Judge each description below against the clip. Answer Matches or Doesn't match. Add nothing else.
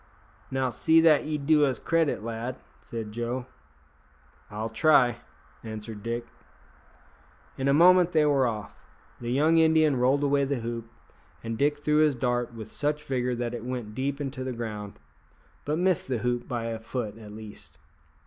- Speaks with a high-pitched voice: Doesn't match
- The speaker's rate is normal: Matches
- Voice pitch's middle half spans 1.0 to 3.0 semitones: Doesn't match